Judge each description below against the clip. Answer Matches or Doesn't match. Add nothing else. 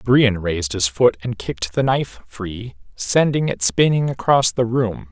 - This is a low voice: Matches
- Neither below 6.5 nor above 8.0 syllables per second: Doesn't match